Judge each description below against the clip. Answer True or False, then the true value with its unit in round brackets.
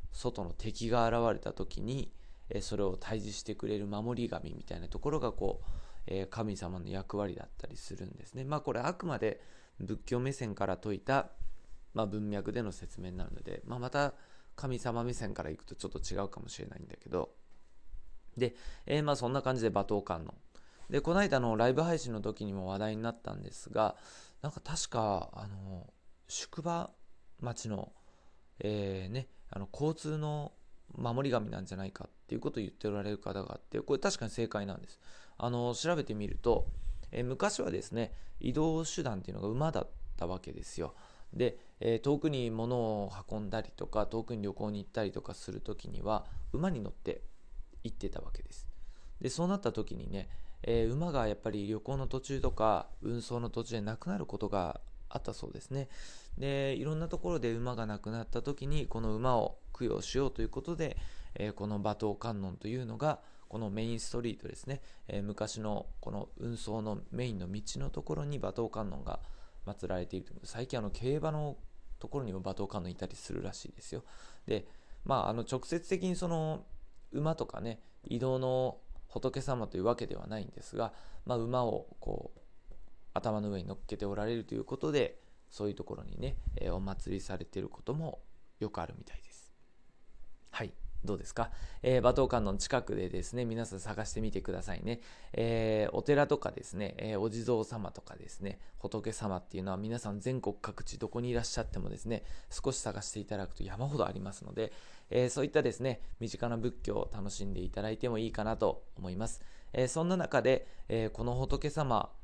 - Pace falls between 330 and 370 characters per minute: True (365 characters per minute)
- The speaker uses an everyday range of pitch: True (4.5 semitones)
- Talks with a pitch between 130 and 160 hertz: False (110 Hz)